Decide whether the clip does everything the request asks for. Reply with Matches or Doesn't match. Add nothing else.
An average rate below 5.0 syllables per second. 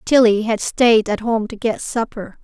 Matches